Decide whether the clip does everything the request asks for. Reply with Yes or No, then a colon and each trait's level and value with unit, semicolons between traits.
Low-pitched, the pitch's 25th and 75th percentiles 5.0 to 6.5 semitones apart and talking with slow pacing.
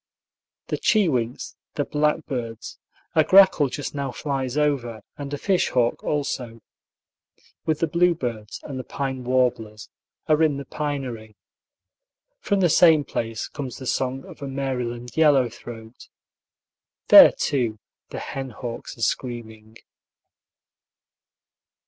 No: low, 130 Hz; average, 3.8 semitones; slow, 125 wpm